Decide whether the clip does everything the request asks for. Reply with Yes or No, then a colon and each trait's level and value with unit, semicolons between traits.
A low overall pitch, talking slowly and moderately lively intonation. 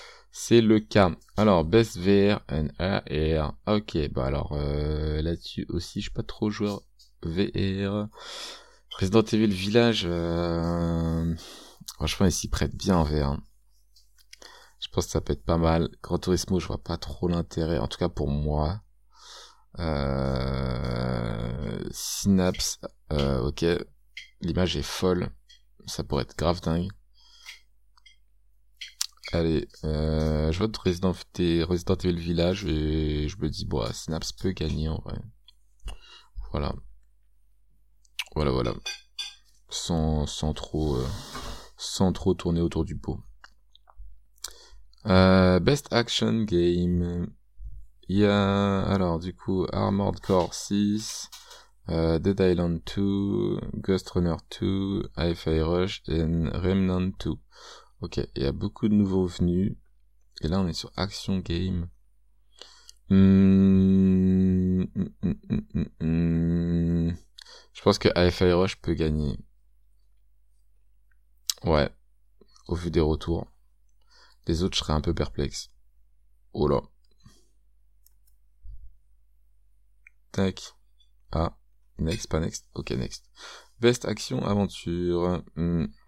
Yes: very low, 85 Hz; slow, 120 wpm; average, 5.0 semitones